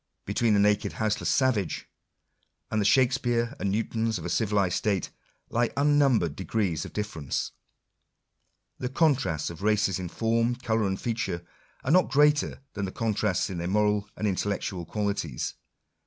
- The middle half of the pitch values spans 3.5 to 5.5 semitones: Yes, average, 3.8 semitones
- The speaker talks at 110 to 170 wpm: Yes, average, 150 wpm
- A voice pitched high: No, low, 105 Hz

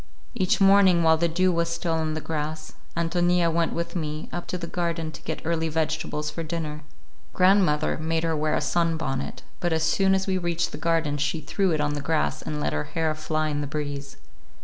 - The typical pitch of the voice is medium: Yes, medium, 160 Hz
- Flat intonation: Yes, narrow, 2.0 semitones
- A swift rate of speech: Yes, fast, 215 wpm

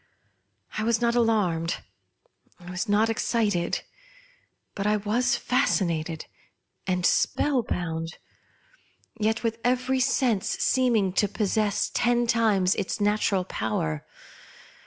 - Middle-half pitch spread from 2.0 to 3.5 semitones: No, average, 4.4 semitones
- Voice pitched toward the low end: No, high, 210 Hz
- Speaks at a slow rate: Yes, slow, 105 wpm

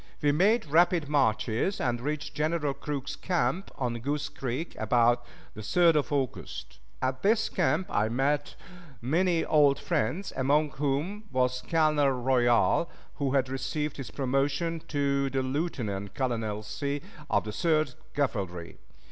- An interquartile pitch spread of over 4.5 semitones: No, average, 3.6 semitones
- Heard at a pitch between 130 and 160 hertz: Yes, medium, 140 Hz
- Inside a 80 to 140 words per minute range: Yes, slow, 135 wpm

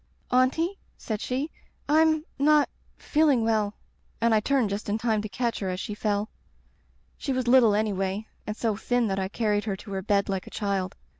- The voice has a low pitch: No, high, 220 Hz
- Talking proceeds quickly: Yes, fast, 215 wpm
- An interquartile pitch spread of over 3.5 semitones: Yes, average, 4.0 semitones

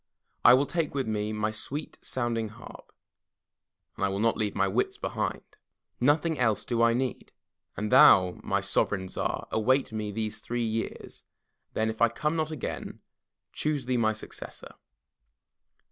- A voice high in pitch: No, low, 115 Hz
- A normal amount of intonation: Yes, average, 3.4 semitones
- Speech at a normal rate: Yes, average, 160 wpm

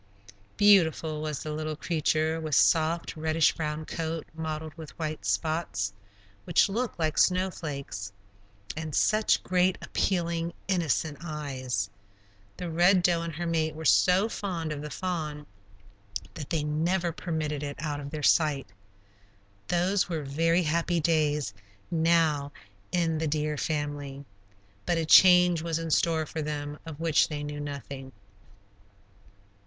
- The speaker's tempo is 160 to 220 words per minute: No, average, 140 wpm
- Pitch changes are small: Yes, narrow, 2.2 semitones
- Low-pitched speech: No, medium, 160 Hz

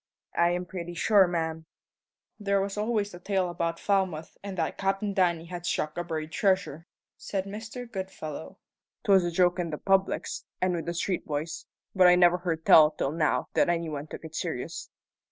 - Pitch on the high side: No, medium, 175 Hz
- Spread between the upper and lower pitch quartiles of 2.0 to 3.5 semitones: Yes, average, 2.9 semitones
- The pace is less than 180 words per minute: No, average, 185 wpm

